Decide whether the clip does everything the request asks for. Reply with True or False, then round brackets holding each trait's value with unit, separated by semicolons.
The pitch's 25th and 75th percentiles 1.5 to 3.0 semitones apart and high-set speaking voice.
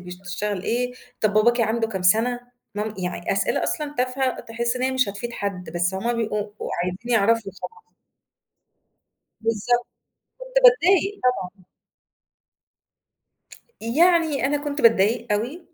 False (4.2 semitones; 230 Hz)